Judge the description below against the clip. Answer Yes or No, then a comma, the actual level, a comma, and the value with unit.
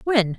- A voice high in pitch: Yes, high, 235 Hz